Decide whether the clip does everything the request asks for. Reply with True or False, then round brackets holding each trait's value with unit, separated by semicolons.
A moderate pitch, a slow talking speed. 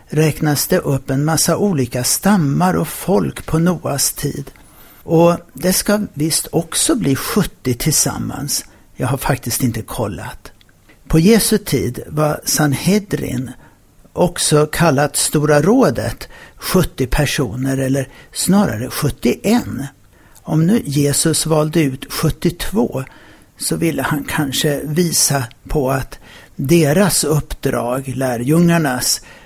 True (150 Hz; 110 wpm)